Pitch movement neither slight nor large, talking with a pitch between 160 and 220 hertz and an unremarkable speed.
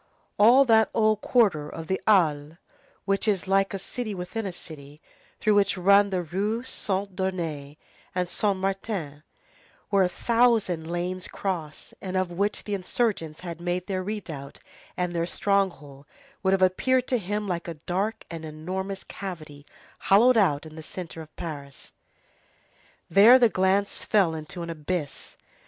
Yes: average, 3.8 semitones; medium, 185 Hz; average, 155 wpm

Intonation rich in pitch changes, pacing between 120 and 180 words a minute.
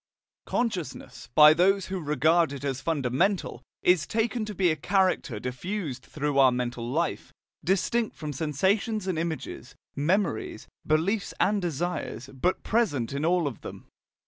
Yes: wide, 5.7 semitones; average, 145 wpm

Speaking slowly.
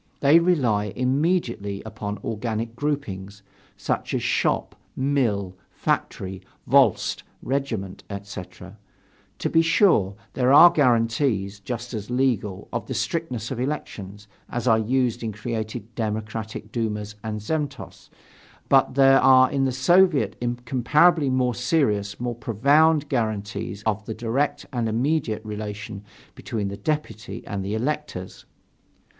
Yes: slow, 125 wpm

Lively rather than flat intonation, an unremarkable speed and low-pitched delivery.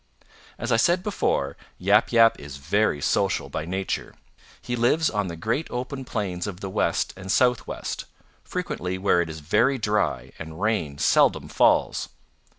Yes: wide, 6.0 semitones; average, 155 wpm; low, 100 Hz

